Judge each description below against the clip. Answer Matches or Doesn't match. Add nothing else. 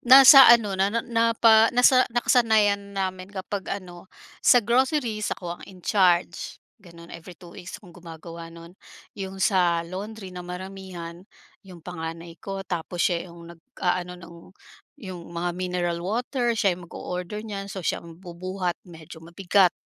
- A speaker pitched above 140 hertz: Matches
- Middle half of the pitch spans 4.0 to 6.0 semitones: Doesn't match